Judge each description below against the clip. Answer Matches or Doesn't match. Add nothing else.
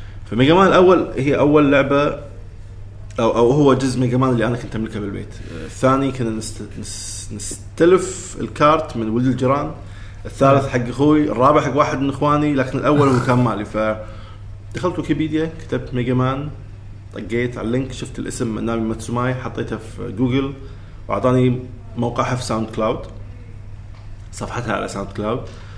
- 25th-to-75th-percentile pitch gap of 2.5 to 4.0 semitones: Doesn't match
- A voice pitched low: Matches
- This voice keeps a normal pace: Doesn't match